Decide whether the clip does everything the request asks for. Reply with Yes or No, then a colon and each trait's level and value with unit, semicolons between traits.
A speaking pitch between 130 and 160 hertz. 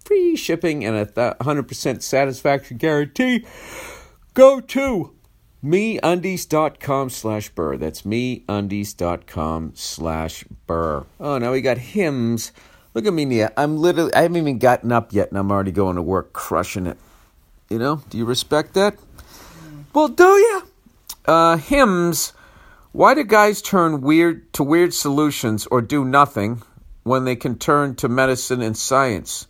Yes: low, 135 Hz